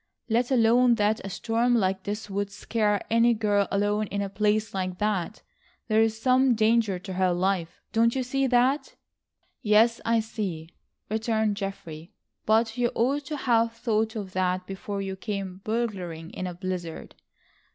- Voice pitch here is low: No, high, 215 Hz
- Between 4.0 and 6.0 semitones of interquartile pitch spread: No, average, 3.1 semitones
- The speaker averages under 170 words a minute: Yes, average, 160 wpm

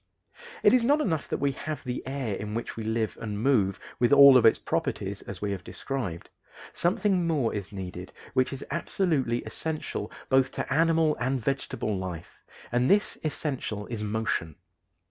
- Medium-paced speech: Yes, average, 170 wpm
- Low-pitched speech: Yes, low, 125 Hz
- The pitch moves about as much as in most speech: No, wide, 6.3 semitones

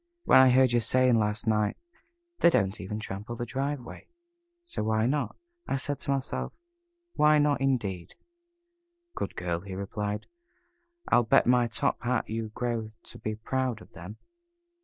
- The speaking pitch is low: Yes, low, 115 Hz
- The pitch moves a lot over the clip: No, average, 3.7 semitones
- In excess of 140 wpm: Yes, average, 160 wpm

